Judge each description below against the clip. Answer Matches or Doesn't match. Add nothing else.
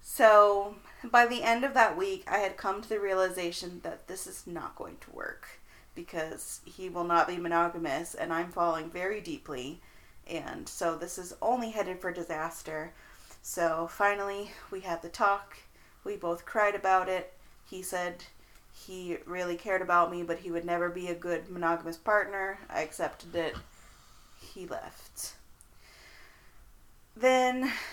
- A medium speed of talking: Matches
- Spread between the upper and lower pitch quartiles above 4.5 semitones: Doesn't match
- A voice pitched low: Doesn't match